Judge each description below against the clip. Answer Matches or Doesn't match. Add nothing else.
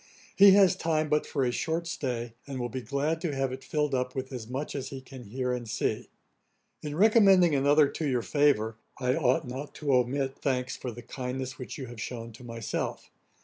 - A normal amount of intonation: Matches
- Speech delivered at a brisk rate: Matches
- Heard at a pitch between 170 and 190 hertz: Doesn't match